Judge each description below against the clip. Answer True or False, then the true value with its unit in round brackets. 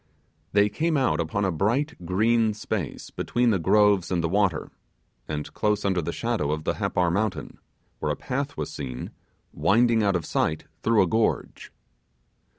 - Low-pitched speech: True (100 Hz)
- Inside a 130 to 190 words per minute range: True (165 wpm)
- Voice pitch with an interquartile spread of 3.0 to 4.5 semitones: False (5.1 semitones)